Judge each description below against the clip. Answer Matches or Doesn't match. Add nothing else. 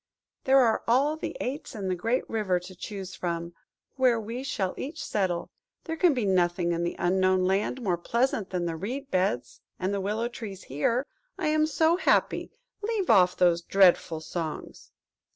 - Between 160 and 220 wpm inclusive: Matches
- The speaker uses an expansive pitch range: Matches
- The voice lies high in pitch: Matches